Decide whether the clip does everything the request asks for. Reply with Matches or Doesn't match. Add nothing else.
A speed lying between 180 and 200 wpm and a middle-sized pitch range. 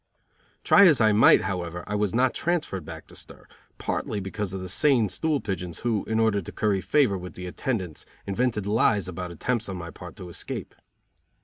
Matches